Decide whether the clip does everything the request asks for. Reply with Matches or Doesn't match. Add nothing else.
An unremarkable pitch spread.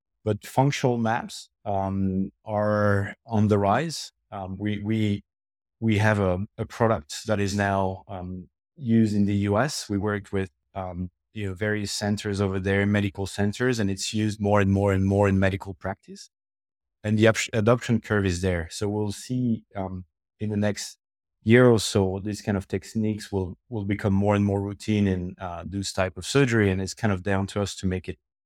Doesn't match